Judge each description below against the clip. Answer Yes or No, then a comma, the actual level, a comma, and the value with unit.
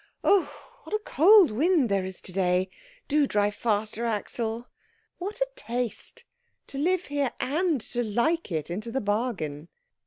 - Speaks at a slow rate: No, average, 155 wpm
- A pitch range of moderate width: No, wide, 7.3 semitones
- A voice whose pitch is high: Yes, high, 235 Hz